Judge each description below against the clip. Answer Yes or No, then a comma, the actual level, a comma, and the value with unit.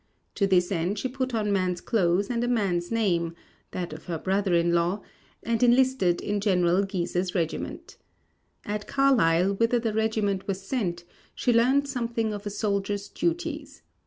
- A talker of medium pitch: No, high, 200 Hz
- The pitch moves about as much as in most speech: Yes, average, 4.4 semitones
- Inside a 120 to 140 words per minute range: No, average, 160 wpm